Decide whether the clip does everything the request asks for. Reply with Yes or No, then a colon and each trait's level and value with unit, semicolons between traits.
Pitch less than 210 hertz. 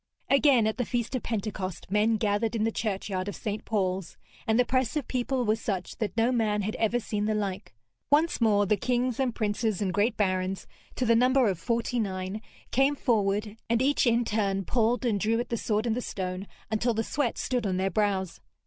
No: high, 220 Hz